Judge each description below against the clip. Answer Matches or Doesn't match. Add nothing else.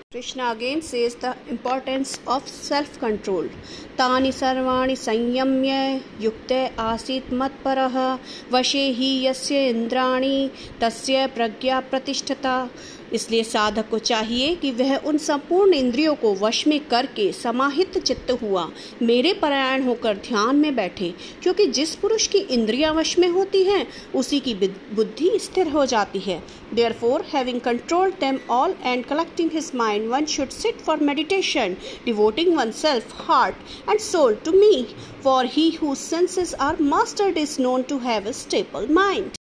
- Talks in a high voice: Matches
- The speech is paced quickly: Doesn't match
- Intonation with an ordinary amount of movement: Matches